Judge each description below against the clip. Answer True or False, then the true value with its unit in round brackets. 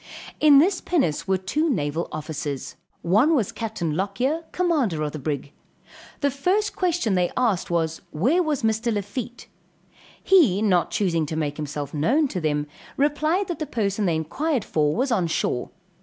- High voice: True (205 Hz)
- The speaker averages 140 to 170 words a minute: True (165 wpm)